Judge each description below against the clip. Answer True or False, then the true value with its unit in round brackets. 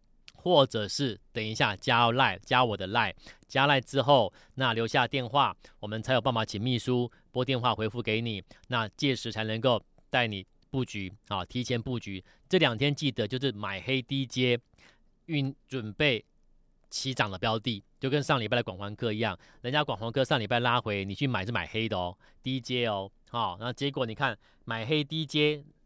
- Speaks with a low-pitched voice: True (120 Hz)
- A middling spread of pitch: True (3.6 semitones)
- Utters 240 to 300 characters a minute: True (265 characters per minute)